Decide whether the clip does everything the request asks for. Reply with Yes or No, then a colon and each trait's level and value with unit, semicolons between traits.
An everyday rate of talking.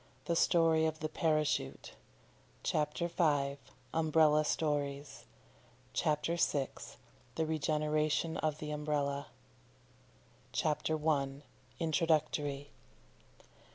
No: slow, 85 wpm